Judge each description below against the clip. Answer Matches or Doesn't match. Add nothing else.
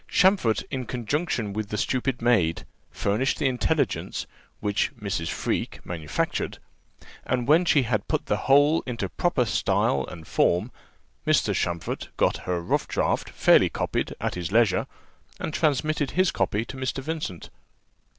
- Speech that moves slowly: Doesn't match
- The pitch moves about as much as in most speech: Doesn't match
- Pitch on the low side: Matches